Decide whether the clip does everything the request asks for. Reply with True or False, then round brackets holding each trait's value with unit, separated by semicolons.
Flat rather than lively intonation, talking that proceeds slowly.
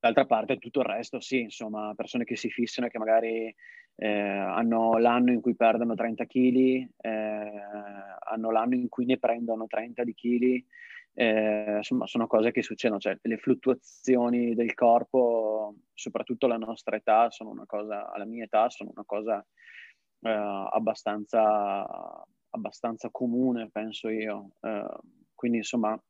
False (2.0 semitones; 145 wpm)